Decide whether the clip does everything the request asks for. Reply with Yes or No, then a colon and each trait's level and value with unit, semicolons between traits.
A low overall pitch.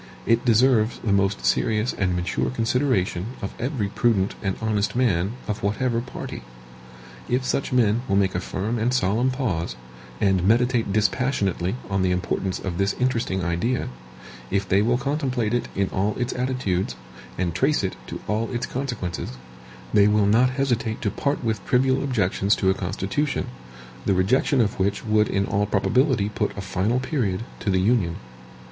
Yes: low, 105 Hz